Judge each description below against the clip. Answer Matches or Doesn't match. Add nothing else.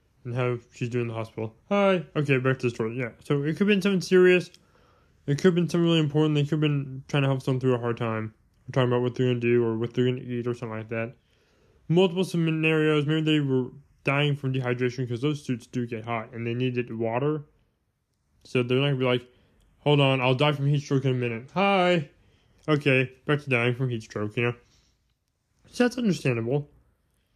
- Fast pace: Matches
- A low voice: Matches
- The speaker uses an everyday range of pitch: Matches